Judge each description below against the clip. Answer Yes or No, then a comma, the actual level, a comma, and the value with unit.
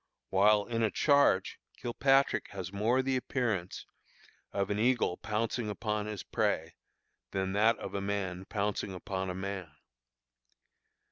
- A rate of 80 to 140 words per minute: Yes, slow, 135 wpm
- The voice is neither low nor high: No, low, 105 Hz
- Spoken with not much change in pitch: No, average, 3.1 semitones